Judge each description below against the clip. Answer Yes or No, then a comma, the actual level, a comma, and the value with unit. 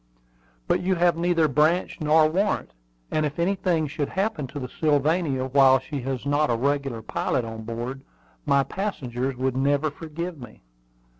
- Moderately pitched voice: Yes, medium, 145 Hz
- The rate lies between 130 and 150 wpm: No, average, 160 wpm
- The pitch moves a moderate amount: Yes, average, 4.0 semitones